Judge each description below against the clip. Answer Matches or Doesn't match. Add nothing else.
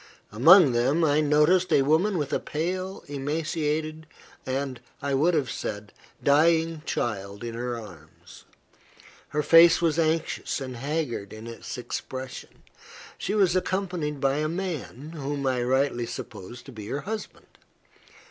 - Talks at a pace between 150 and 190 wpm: Doesn't match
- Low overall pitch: Doesn't match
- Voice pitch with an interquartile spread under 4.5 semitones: Doesn't match